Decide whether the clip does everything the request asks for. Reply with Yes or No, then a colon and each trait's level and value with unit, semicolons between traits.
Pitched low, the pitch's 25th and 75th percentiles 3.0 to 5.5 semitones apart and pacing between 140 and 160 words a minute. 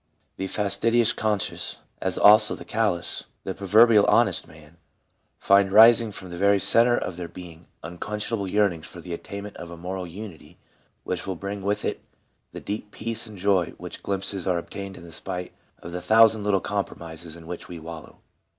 No: very low, 95 Hz; average, 3.4 semitones; average, 180 wpm